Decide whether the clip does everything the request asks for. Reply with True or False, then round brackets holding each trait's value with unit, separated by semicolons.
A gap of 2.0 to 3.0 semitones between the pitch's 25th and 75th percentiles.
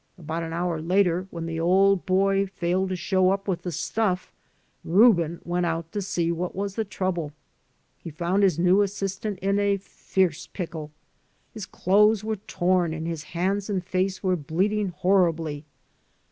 True (2.7 semitones)